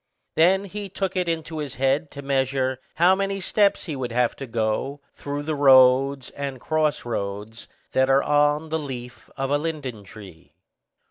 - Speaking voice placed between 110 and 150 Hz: Yes, medium, 140 Hz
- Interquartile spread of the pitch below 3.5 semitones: No, average, 3.8 semitones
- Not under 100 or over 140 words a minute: No, average, 175 wpm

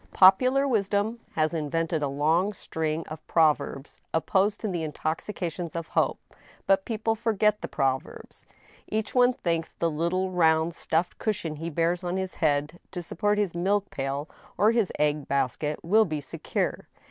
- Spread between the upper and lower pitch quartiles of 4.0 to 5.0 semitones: Yes, average, 4.7 semitones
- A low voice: No, medium, 170 Hz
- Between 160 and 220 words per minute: Yes, average, 170 wpm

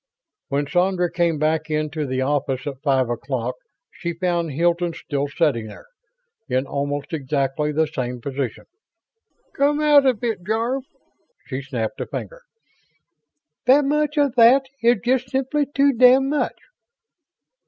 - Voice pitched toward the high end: No, medium, 165 Hz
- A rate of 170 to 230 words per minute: No, average, 140 wpm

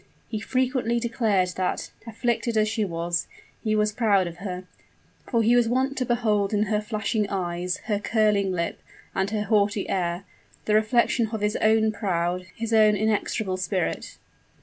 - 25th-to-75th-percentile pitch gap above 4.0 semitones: No, average, 2.8 semitones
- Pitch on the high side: Yes, high, 210 Hz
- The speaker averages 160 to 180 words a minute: Yes, average, 165 wpm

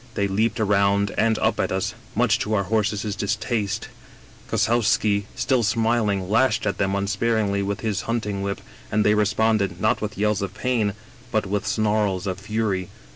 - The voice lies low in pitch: Yes, low, 105 Hz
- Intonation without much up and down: Yes, narrow, 1.8 semitones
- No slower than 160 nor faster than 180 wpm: Yes, average, 165 wpm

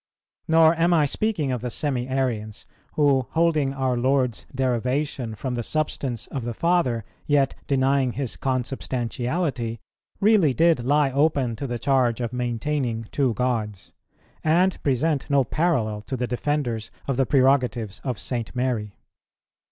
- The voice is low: Yes, low, 130 Hz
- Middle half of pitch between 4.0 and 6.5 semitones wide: No, average, 3.5 semitones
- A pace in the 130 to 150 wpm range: Yes, average, 145 wpm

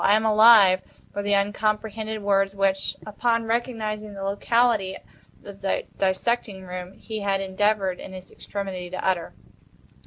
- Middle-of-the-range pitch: No, high, 200 Hz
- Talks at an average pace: Yes, average, 145 wpm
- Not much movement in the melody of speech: Yes, narrow, 2.1 semitones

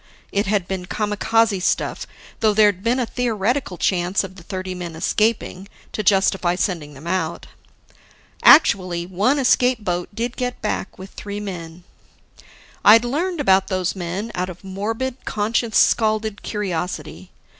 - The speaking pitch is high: Yes, high, 200 Hz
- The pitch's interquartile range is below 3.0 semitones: No, average, 3.7 semitones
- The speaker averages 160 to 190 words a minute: No, average, 145 wpm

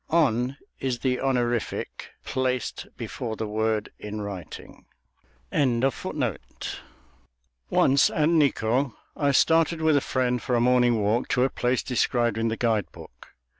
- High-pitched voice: No, low, 125 Hz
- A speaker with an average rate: No, slow, 130 wpm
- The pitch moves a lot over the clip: No, average, 3.4 semitones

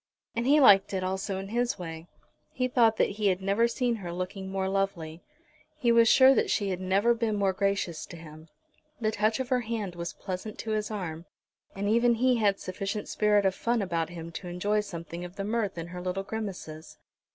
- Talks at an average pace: No, fast, 210 wpm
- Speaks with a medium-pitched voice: No, high, 195 Hz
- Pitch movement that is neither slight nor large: Yes, average, 3.6 semitones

